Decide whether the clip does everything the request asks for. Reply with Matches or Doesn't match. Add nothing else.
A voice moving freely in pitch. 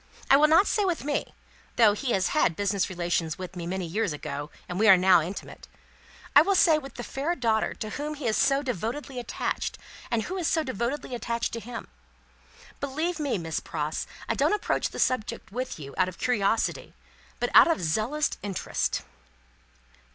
Matches